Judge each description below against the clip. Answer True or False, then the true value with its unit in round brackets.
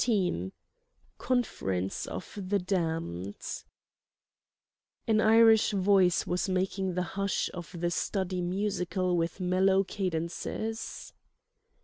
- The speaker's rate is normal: False (95 wpm)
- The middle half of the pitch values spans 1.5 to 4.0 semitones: True (2.6 semitones)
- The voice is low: False (185 Hz)